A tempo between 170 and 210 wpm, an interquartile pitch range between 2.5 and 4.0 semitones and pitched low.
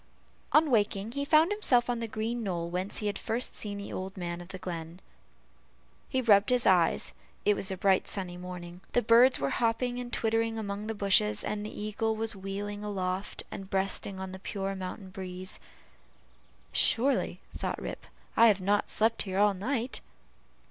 No: average, 175 wpm; average, 3.3 semitones; high, 205 Hz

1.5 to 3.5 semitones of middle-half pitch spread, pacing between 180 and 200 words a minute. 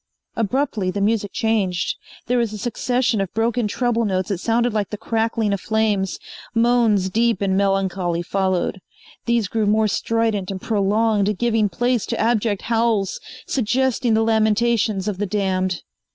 No: average, 2.9 semitones; average, 150 wpm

